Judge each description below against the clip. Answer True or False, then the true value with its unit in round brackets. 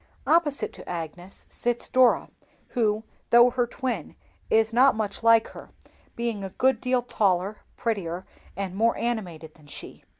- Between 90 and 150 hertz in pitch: False (225 Hz)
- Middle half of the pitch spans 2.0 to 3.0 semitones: False (4.3 semitones)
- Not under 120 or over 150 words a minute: True (145 wpm)